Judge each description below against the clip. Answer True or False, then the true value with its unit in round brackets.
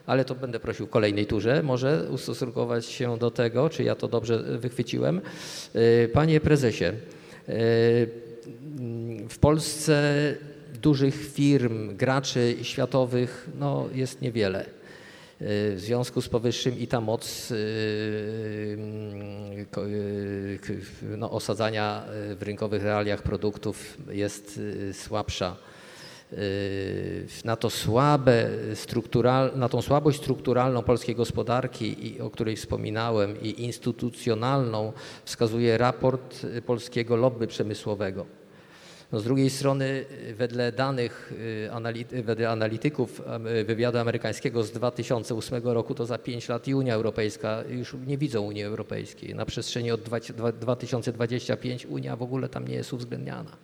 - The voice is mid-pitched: False (120 Hz)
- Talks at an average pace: False (105 wpm)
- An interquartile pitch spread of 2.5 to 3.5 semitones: True (3.1 semitones)